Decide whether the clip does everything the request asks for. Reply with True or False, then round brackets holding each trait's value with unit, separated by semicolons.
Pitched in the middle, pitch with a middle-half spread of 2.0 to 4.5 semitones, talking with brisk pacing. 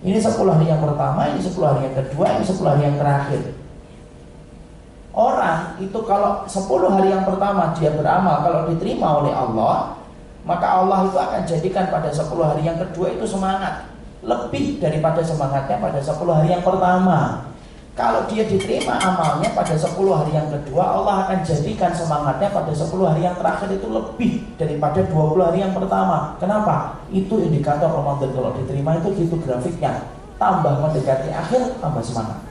True (170 Hz; 3.9 semitones; 160 wpm)